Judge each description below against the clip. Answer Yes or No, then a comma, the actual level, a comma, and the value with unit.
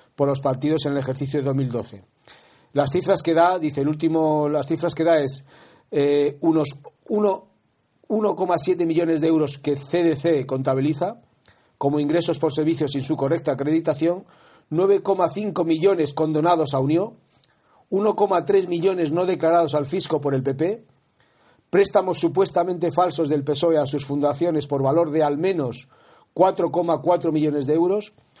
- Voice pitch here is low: No, medium, 160 Hz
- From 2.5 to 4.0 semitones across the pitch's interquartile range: Yes, average, 3.5 semitones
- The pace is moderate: Yes, average, 145 wpm